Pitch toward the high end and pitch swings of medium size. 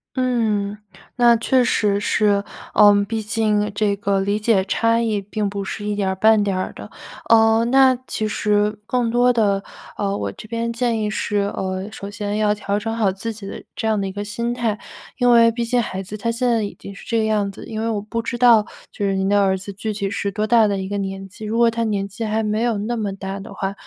No: high, 210 Hz; narrow, 2.3 semitones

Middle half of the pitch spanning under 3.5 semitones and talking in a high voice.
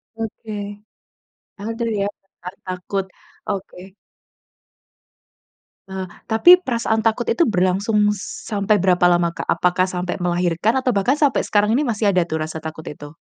No: average, 3.8 semitones; high, 195 Hz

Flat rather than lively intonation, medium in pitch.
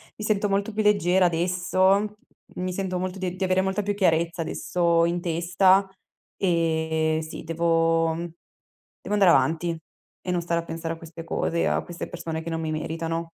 Yes: narrow, 2.3 semitones; medium, 170 Hz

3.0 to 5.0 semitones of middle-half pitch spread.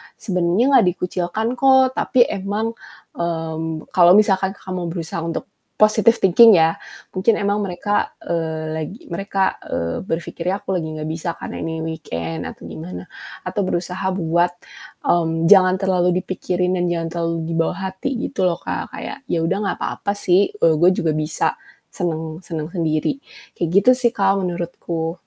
Yes: average, 3.3 semitones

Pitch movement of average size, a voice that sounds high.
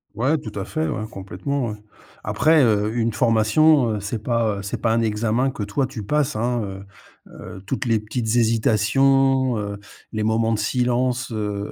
No: average, 3.3 semitones; low, 115 Hz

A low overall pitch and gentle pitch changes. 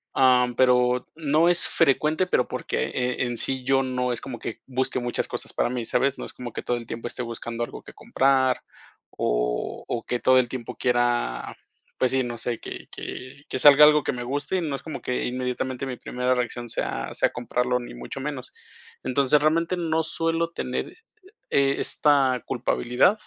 Yes: low, 130 Hz; narrow, 2.3 semitones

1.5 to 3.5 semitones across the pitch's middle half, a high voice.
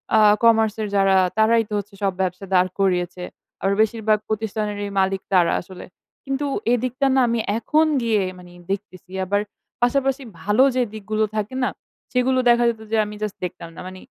Yes: average, 3.2 semitones; high, 215 Hz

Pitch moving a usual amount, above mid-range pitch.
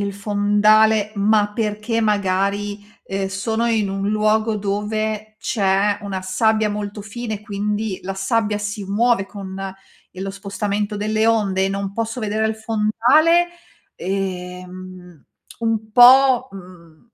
No: narrow, 1.9 semitones; high, 210 Hz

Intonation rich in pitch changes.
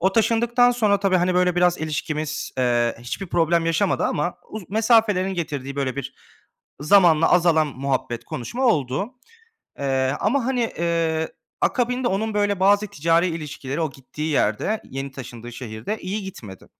Yes: wide, 6.6 semitones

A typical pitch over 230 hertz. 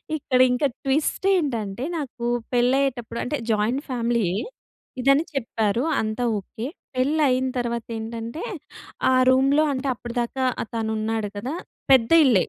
Yes: high, 245 Hz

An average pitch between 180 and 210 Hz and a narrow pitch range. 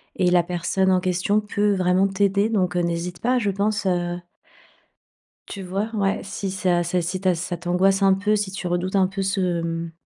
Yes: medium, 185 Hz; narrow, 2.0 semitones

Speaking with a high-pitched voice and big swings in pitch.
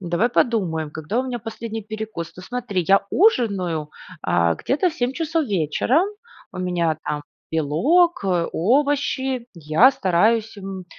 Yes: high, 205 Hz; wide, 6.7 semitones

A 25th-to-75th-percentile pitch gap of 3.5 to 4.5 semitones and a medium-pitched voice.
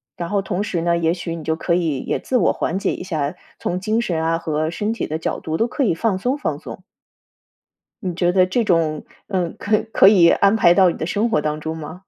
Yes: average, 3.9 semitones; medium, 175 Hz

